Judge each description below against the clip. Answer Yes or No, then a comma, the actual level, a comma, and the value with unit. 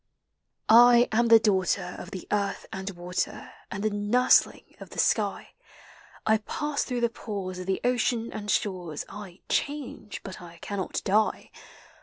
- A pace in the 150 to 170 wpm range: Yes, average, 155 wpm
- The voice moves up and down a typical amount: Yes, average, 3.7 semitones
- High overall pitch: Yes, high, 205 Hz